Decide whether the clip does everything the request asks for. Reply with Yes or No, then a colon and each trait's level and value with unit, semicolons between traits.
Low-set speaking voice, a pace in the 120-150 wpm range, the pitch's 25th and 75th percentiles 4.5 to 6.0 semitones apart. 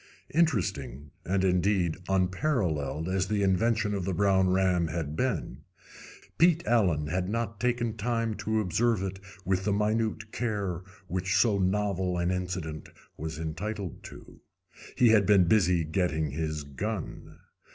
No: very low, 95 Hz; average, 140 wpm; average, 3.7 semitones